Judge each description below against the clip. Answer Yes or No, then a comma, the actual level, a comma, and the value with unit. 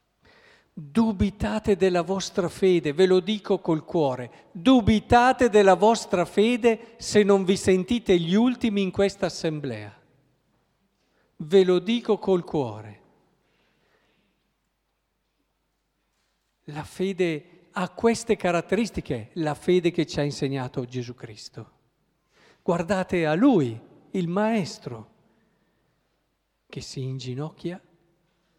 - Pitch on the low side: No, medium, 185 Hz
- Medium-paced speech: No, slow, 100 wpm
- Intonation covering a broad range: No, average, 4.7 semitones